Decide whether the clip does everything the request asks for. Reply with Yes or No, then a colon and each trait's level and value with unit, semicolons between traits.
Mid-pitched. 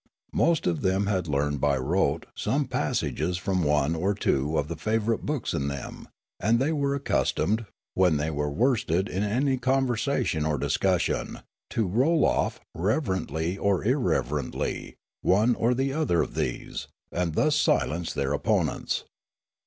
No: very low, 95 Hz